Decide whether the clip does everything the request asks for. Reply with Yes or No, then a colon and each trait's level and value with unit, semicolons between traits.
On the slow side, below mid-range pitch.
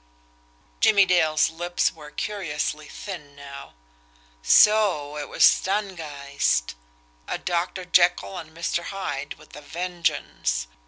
No: slow, 110 wpm; medium, 165 Hz